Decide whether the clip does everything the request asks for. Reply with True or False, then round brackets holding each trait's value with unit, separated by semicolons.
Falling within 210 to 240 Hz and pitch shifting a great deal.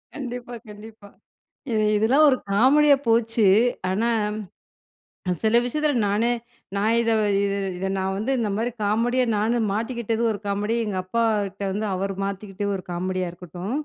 False (215 Hz; 3.1 semitones)